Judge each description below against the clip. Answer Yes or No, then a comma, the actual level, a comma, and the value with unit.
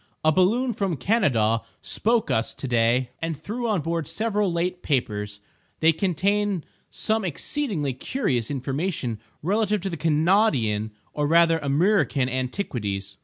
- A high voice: No, medium, 165 Hz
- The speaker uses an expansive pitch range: Yes, wide, 7.8 semitones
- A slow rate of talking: Yes, slow, 125 wpm